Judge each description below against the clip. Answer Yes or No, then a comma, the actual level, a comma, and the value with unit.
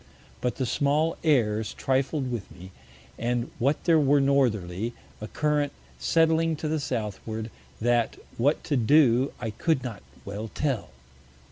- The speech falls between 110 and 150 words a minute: Yes, average, 140 wpm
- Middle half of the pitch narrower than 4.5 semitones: No, average, 4.9 semitones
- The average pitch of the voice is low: Yes, low, 130 Hz